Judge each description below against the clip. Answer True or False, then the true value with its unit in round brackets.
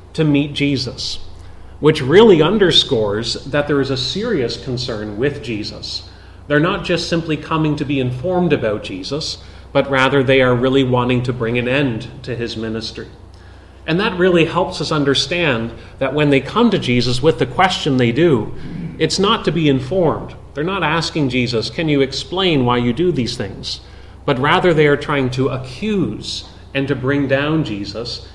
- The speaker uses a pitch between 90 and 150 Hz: True (135 Hz)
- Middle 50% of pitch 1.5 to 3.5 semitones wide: False (5.1 semitones)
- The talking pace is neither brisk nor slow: True (175 wpm)